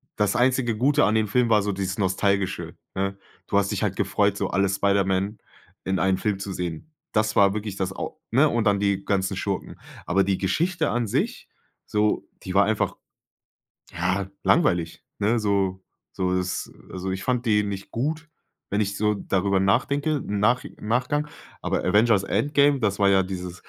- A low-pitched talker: Yes, low, 100 Hz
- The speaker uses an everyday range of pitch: Yes, average, 3.1 semitones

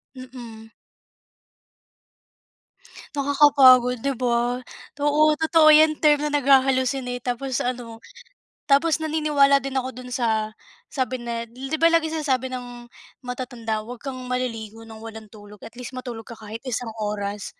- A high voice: Yes, very high, 250 Hz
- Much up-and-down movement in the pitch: No, average, 3.3 semitones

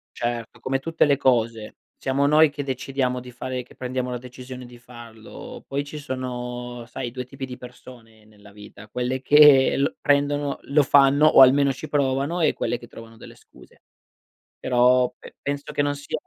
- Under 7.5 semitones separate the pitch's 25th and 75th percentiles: Yes, narrow, 2.5 semitones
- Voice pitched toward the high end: No, low, 130 Hz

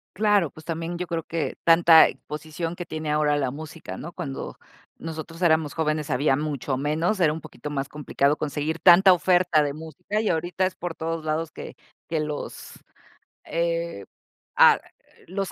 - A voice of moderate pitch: Yes, medium, 160 Hz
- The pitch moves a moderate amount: No, narrow, 2.3 semitones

